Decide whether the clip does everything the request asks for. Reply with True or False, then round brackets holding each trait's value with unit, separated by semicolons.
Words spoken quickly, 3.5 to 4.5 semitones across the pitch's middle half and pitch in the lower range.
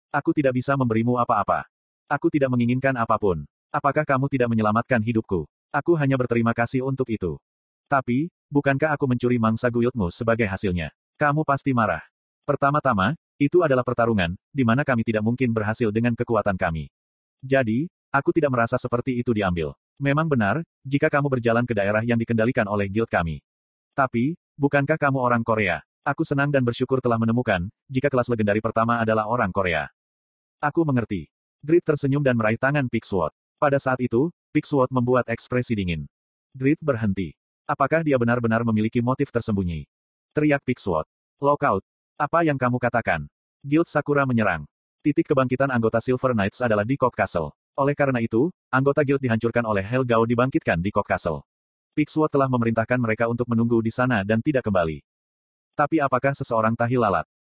True (155 wpm; 4.0 semitones; 120 Hz)